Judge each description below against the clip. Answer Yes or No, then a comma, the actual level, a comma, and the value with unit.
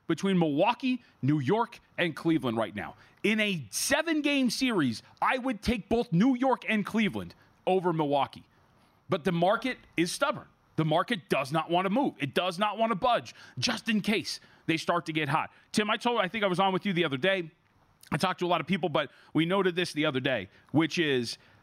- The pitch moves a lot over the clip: Yes, wide, 6.0 semitones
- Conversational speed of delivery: No, fast, 215 wpm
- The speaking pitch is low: No, medium, 185 Hz